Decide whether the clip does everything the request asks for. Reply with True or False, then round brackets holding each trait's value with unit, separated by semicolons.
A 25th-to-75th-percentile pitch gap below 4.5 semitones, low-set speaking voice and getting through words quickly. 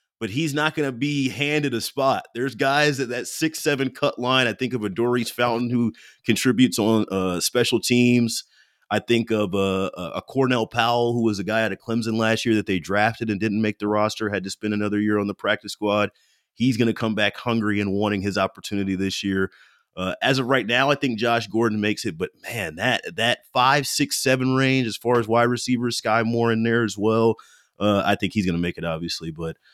True (3.4 semitones; 115 Hz; 230 wpm)